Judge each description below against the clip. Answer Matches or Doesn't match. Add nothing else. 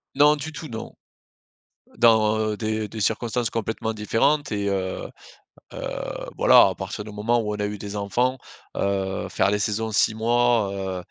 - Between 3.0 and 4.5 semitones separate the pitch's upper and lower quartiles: Doesn't match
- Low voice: Matches